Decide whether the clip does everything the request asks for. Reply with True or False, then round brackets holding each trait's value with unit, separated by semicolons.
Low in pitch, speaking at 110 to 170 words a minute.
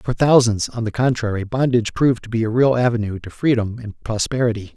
False (115 Hz; 200 wpm)